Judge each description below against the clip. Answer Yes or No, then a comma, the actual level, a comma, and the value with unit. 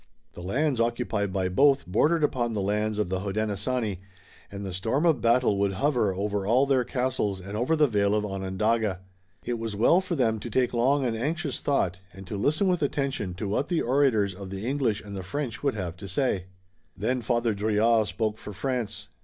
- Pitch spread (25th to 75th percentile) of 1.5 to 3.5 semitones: No, average, 4.6 semitones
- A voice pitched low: Yes, low, 110 Hz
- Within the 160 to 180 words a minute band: No, fast, 205 wpm